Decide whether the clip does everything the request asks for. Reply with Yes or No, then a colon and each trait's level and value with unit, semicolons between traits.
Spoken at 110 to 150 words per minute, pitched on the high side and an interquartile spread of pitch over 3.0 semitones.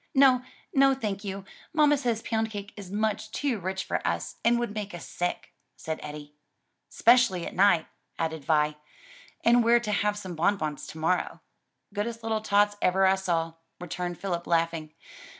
No: average, 170 wpm; high, 200 Hz; average, 4.7 semitones